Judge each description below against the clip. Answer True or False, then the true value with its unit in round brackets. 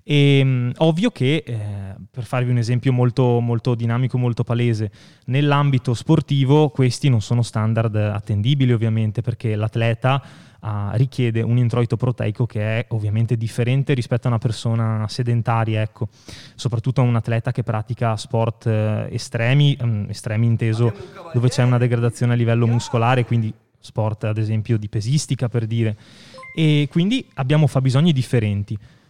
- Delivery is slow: False (140 wpm)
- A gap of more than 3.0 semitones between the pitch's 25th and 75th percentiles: False (2.4 semitones)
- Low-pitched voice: True (120 Hz)